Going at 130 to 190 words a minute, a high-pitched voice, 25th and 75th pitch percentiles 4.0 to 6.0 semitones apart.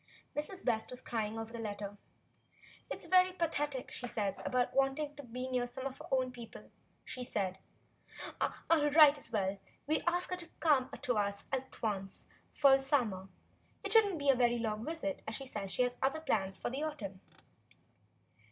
No: fast, 205 wpm; very high, 255 Hz; average, 5.1 semitones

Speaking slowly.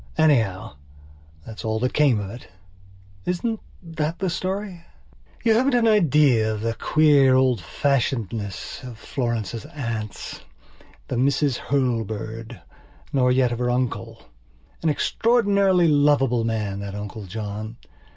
Yes: slow, 125 wpm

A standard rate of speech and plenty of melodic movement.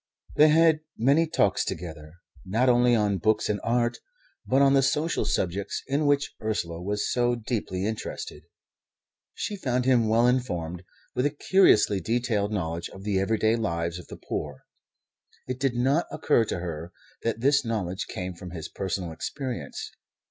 Yes: average, 160 wpm; wide, 5.7 semitones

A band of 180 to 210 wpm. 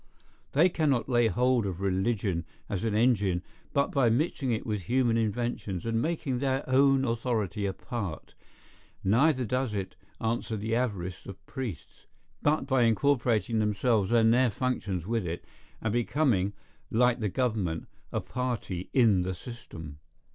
No: average, 145 wpm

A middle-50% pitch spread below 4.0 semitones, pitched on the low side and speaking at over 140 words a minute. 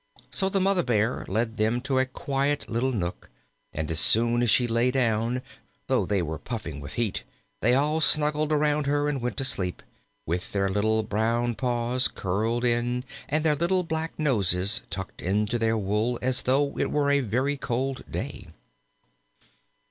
No: average, 4.5 semitones; low, 120 Hz; average, 170 wpm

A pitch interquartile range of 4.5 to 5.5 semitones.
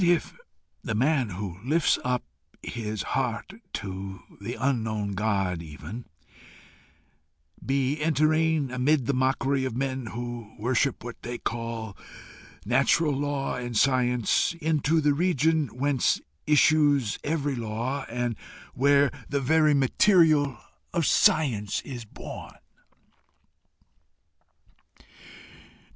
No: average, 4.1 semitones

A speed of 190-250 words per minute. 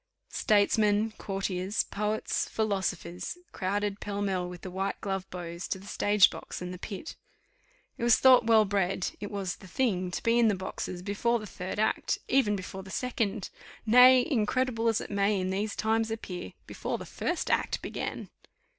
No: average, 175 wpm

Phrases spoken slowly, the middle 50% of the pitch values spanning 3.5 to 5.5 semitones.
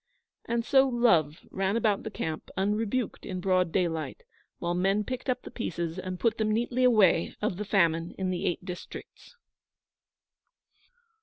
No: average, 155 wpm; average, 4.5 semitones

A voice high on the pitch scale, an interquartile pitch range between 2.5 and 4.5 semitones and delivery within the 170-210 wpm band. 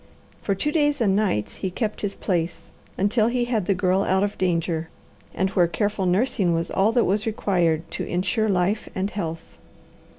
Yes: high, 195 Hz; average, 3.3 semitones; average, 185 wpm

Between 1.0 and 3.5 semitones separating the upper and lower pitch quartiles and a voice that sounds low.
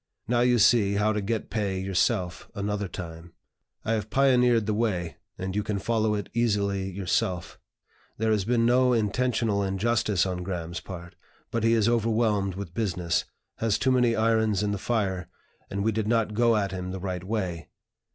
Yes: average, 3.2 semitones; low, 105 Hz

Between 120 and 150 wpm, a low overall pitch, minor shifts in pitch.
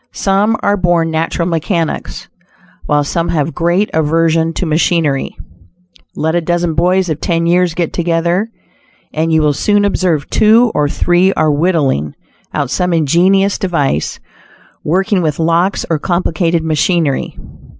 No: average, 140 wpm; medium, 170 Hz; narrow, 2.3 semitones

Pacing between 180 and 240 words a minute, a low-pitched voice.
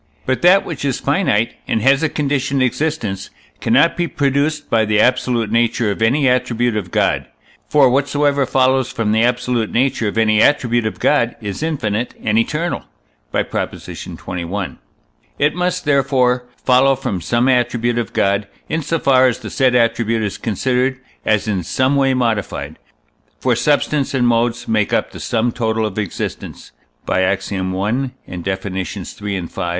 No: average, 165 wpm; low, 120 Hz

